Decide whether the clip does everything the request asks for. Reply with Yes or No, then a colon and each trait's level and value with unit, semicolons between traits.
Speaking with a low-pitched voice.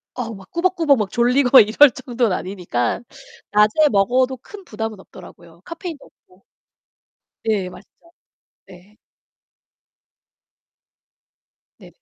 No: high, 225 Hz